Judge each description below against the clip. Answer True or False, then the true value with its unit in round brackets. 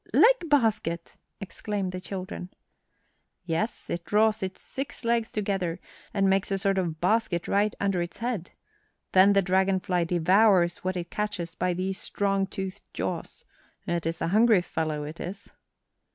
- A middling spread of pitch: True (3.0 semitones)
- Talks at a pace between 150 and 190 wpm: True (155 wpm)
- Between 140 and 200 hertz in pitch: True (190 Hz)